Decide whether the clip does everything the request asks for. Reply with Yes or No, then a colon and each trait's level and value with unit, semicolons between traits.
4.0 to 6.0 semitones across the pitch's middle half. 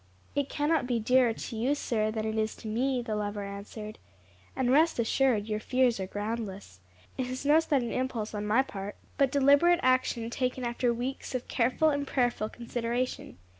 No: average, 3.4 semitones